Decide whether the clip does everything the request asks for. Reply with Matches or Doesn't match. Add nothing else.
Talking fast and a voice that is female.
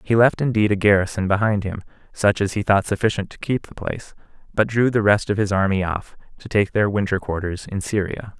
Doesn't match